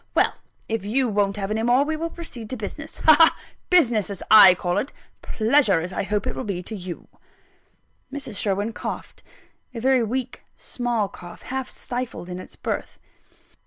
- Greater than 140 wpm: Yes, average, 175 wpm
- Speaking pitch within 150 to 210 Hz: No, high, 220 Hz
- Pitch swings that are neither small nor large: Yes, average, 4.7 semitones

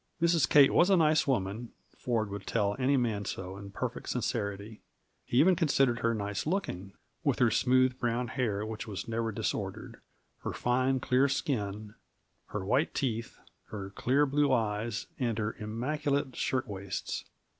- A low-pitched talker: Yes, low, 120 Hz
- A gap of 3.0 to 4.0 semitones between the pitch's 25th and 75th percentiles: No, average, 4.5 semitones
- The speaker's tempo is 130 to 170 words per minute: Yes, average, 155 wpm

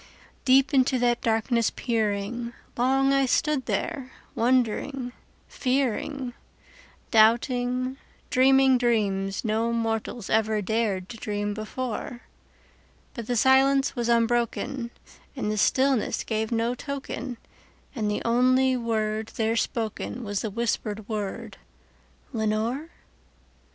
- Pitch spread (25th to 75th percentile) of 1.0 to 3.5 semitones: Yes, average, 2.9 semitones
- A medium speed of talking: No, slow, 100 wpm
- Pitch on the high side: Yes, high, 235 Hz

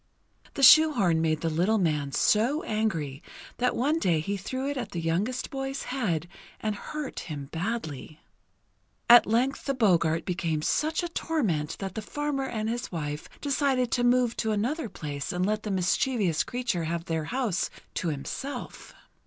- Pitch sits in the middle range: No, high, 215 Hz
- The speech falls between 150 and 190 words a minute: Yes, average, 165 wpm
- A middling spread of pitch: No, wide, 7.7 semitones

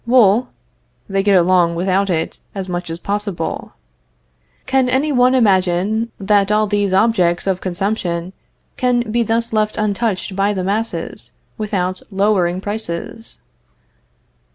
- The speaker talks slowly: Yes, slow, 130 wpm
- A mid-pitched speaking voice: No, high, 200 Hz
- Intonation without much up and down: No, average, 3.2 semitones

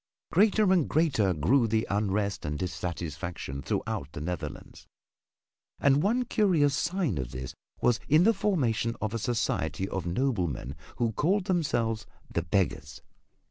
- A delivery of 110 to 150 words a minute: Yes, average, 140 wpm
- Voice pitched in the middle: No, low, 110 Hz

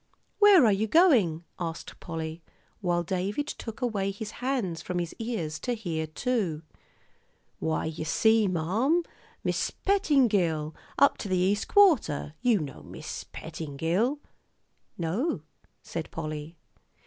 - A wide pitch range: Yes, wide, 7.0 semitones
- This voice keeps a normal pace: No, slow, 125 wpm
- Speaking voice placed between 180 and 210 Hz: Yes, high, 190 Hz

